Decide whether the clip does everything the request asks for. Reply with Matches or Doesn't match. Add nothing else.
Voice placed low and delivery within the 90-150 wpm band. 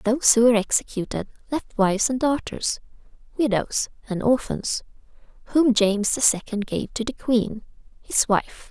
Doesn't match